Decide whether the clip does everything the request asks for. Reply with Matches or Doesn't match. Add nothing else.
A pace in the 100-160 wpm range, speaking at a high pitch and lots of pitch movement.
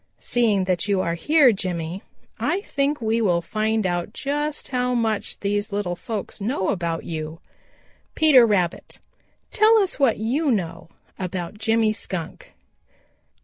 Matches